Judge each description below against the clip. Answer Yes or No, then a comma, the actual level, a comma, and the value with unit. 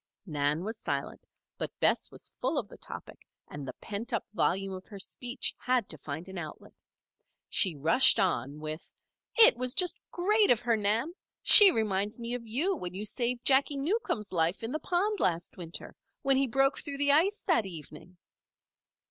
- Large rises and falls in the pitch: Yes, wide, 7.3 semitones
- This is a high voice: Yes, high, 225 Hz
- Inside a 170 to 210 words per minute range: Yes, average, 180 wpm